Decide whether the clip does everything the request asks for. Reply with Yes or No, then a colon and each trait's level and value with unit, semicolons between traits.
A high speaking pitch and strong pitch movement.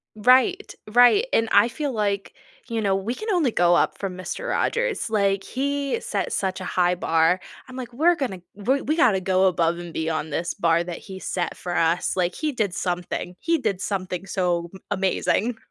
Yes: high, 195 Hz; wide, 6.2 semitones